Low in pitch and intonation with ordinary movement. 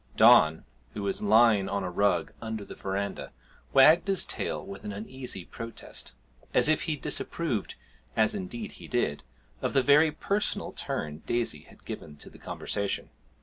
No: low, 110 Hz; wide, 6.9 semitones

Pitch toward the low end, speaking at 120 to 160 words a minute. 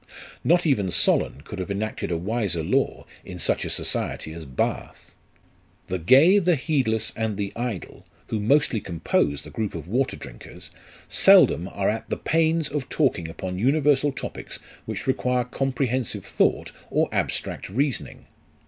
Yes: low, 115 Hz; average, 150 wpm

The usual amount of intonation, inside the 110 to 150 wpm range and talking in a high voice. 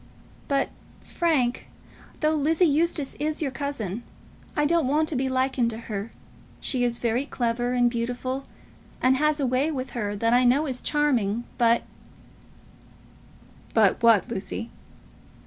Yes: average, 3.8 semitones; average, 145 wpm; very high, 255 Hz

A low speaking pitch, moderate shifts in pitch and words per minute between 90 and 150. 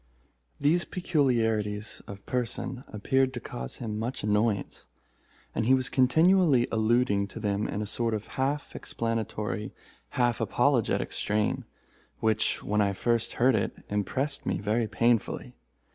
Yes: low, 115 Hz; average, 3.6 semitones; slow, 135 wpm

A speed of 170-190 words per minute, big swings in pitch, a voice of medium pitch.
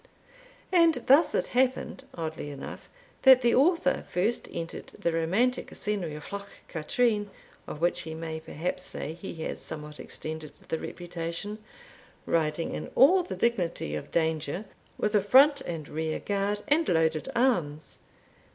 No: average, 145 wpm; wide, 7.3 semitones; medium, 175 Hz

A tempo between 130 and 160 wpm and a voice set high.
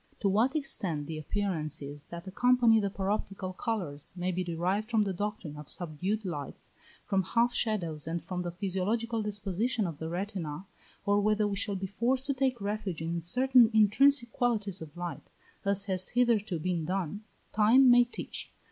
No: average, 170 wpm; high, 200 Hz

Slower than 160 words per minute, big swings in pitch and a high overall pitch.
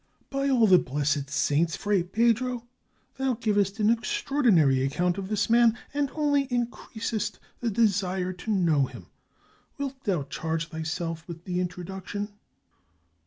Yes: average, 145 wpm; wide, 5.8 semitones; high, 200 Hz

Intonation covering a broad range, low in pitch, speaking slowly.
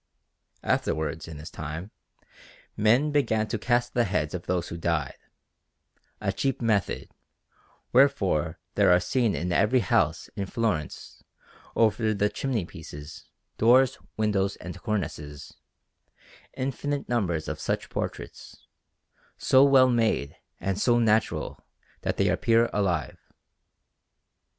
Yes: wide, 6.0 semitones; low, 105 Hz; slow, 120 wpm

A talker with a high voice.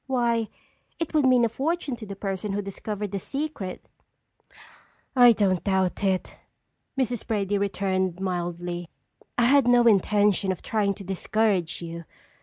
Yes: high, 200 Hz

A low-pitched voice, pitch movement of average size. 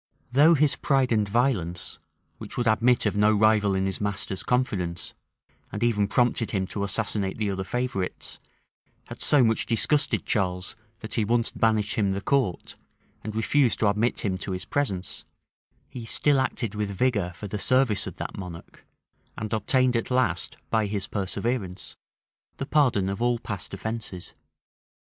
Yes: low, 110 Hz; average, 3.8 semitones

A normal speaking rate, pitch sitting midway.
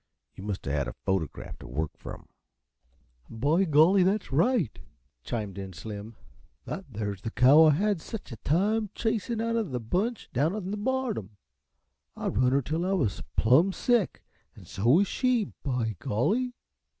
Yes: average, 170 wpm; medium, 155 Hz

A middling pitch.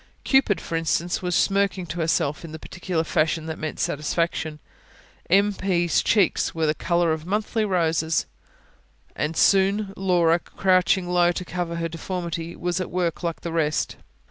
Yes: medium, 170 Hz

